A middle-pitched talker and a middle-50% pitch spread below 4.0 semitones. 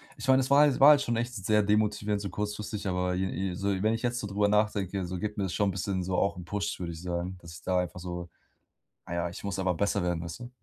No: low, 100 Hz; average, 2.8 semitones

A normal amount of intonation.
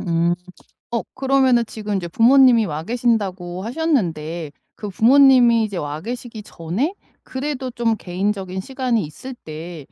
No: wide, 6.2 semitones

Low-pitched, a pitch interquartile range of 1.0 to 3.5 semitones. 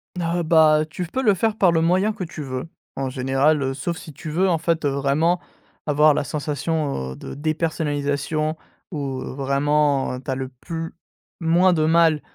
No: medium, 155 Hz; average, 3.1 semitones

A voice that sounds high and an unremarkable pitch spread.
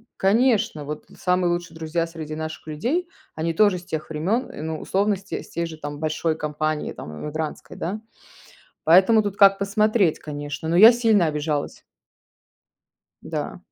No: medium, 165 Hz; average, 4.5 semitones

